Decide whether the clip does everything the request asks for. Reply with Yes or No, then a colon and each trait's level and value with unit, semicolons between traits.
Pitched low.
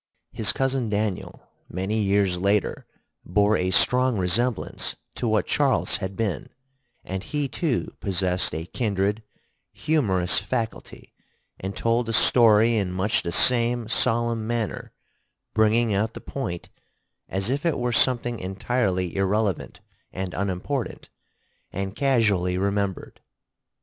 Yes: low, 105 Hz